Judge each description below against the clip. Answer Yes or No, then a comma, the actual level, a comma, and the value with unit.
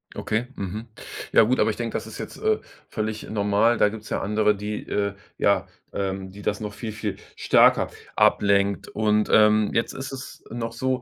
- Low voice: Yes, low, 105 Hz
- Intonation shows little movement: Yes, narrow, 2.0 semitones